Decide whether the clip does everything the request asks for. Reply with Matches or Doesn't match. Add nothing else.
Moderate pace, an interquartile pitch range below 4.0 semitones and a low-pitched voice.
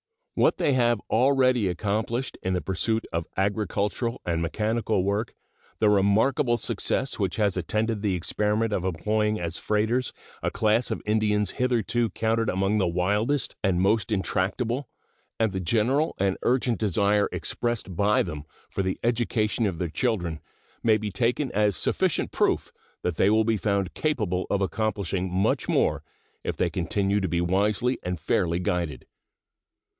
Matches